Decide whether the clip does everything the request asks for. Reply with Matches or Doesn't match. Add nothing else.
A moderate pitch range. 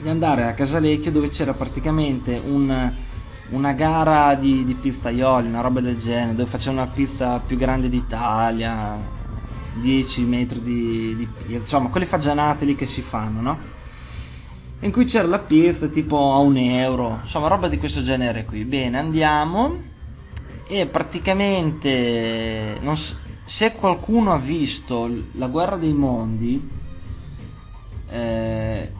Matches